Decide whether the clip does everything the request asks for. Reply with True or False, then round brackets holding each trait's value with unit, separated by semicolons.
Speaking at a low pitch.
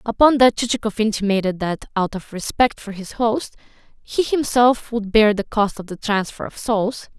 False (220 Hz)